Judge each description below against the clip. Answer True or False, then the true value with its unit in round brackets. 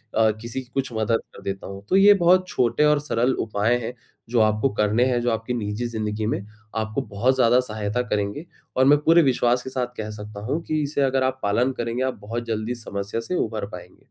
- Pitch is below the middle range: True (120 Hz)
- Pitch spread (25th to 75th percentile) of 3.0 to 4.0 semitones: True (3.4 semitones)